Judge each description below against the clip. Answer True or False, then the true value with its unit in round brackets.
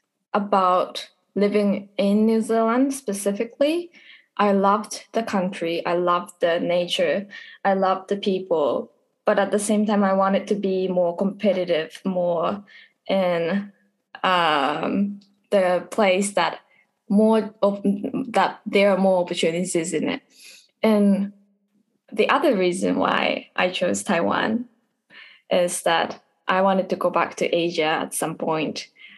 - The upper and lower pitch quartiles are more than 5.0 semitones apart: False (2.6 semitones)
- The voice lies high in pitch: True (200 Hz)